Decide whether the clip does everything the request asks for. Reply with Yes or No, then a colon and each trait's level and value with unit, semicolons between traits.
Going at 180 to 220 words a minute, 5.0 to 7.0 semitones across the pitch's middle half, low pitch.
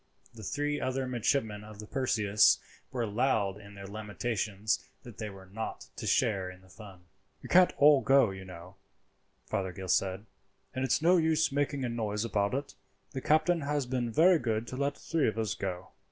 Yes: average, 185 wpm; wide, 5.4 semitones; low, 110 Hz